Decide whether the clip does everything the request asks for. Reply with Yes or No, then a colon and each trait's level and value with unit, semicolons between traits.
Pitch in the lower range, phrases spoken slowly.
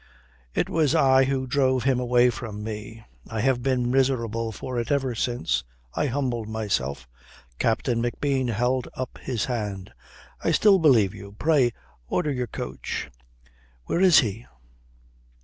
No: low, 120 Hz; average, 145 wpm